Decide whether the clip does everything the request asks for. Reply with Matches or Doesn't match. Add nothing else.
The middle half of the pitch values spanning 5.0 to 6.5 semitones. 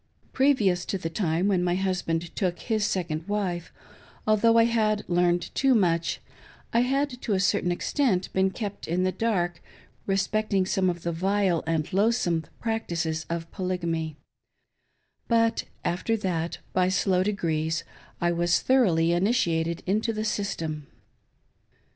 Doesn't match